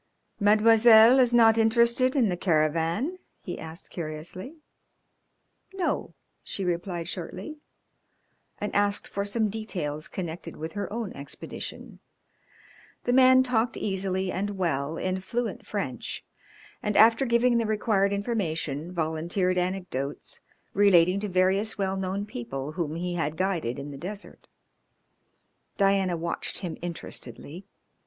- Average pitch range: Yes, average, 4.7 semitones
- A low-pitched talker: No, high, 190 Hz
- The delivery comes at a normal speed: No, slow, 125 wpm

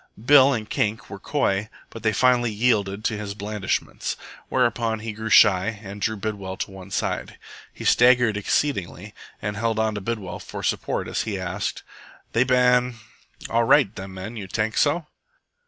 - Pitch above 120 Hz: No, low, 110 Hz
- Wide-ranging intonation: No, average, 2.8 semitones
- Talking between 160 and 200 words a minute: Yes, average, 170 wpm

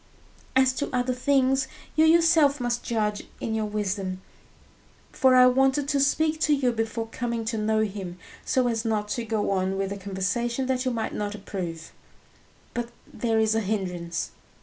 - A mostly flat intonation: No, average, 4.1 semitones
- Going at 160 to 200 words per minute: Yes, average, 170 wpm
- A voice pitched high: Yes, high, 230 Hz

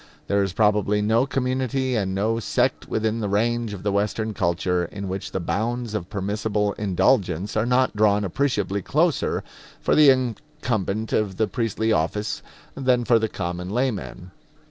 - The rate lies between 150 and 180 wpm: Yes, average, 160 wpm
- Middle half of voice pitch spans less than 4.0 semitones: Yes, average, 3.4 semitones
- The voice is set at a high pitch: No, low, 105 Hz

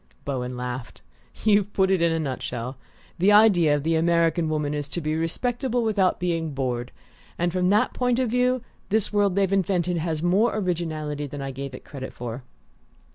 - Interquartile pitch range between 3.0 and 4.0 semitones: No, wide, 5.6 semitones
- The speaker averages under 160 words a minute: No, average, 185 wpm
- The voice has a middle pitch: Yes, medium, 170 Hz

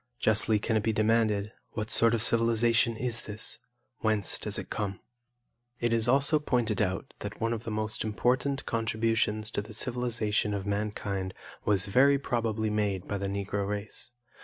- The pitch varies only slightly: Yes, narrow, 2.1 semitones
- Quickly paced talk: No, average, 165 wpm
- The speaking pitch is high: No, low, 110 Hz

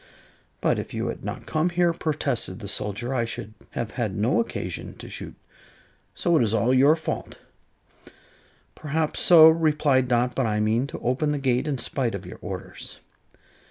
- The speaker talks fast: No, average, 175 wpm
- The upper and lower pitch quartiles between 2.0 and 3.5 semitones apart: No, average, 5.2 semitones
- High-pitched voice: No, low, 130 Hz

